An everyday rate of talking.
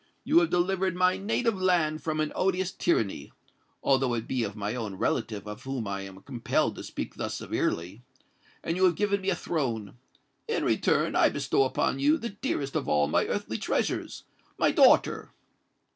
Yes: average, 175 wpm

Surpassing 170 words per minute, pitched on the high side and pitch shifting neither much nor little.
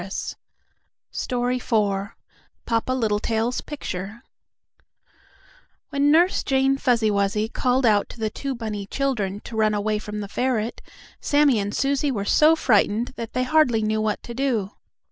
No: slow, 135 wpm; high, 230 Hz; average, 4.1 semitones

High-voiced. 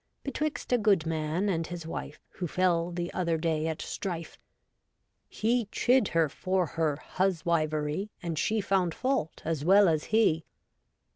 No: medium, 170 Hz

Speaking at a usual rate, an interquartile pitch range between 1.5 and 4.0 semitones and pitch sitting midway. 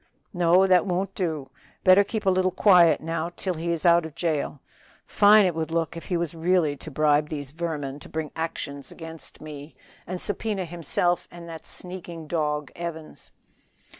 Yes: average, 180 wpm; narrow, 2.6 semitones; medium, 165 Hz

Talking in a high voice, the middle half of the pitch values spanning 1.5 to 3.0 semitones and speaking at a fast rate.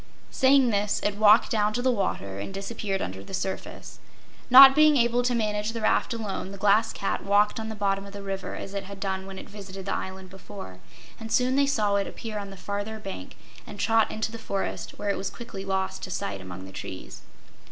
Yes: high, 205 Hz; narrow, 2.5 semitones; fast, 225 wpm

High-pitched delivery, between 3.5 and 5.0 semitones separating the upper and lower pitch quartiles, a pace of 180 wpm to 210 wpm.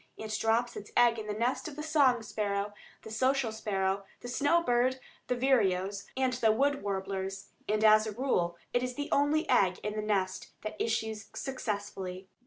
Yes: high, 220 Hz; average, 4.0 semitones; average, 185 wpm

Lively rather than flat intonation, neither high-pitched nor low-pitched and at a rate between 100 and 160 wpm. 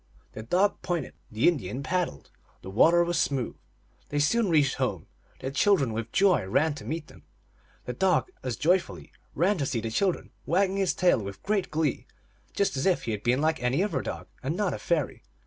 No: wide, 6.6 semitones; medium, 155 Hz; average, 200 wpm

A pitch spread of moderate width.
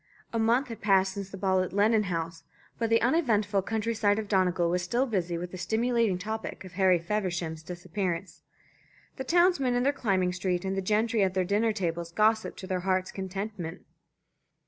Yes: average, 3.4 semitones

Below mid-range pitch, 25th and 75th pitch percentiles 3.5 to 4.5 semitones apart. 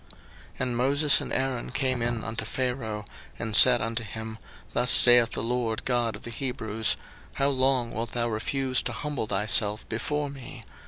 No: low, 120 Hz; average, 2.7 semitones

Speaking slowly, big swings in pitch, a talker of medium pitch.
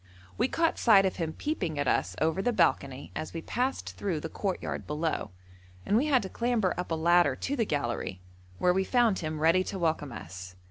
No: fast, 205 wpm; wide, 6.0 semitones; medium, 175 Hz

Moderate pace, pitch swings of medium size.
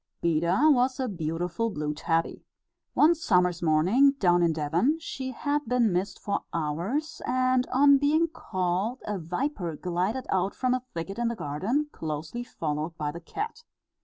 No: average, 160 wpm; wide, 7.6 semitones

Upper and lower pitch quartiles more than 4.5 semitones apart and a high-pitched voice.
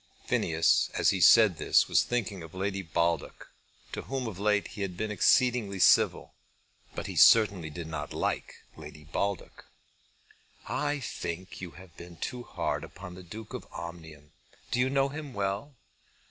No: average, 4.9 semitones; very low, 95 Hz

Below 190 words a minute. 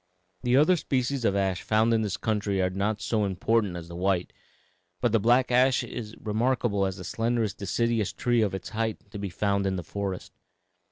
No: average, 200 wpm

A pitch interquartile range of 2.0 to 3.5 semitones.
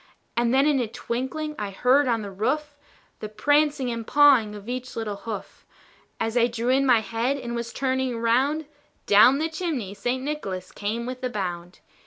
No: average, 4.0 semitones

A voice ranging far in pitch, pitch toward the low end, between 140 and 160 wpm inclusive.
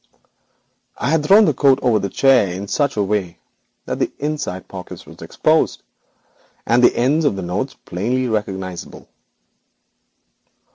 Yes: wide, 6.3 semitones; low, 115 Hz; average, 150 wpm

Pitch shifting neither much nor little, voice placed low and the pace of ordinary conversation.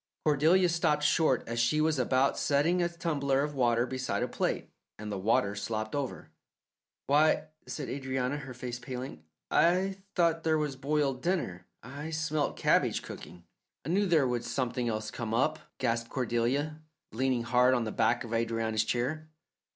Yes: average, 4.6 semitones; low, 130 Hz; average, 165 wpm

